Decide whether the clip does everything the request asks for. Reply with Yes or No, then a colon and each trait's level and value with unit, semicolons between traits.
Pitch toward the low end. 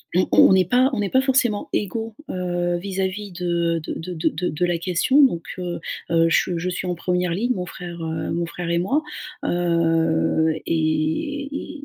No: medium, 180 Hz